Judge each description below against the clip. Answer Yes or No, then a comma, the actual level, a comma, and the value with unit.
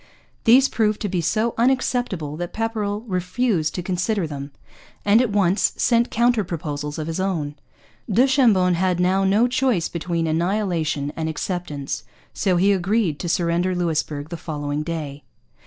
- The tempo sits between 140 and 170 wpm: Yes, average, 155 wpm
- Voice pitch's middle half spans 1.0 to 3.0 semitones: No, average, 4.9 semitones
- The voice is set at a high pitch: No, medium, 180 Hz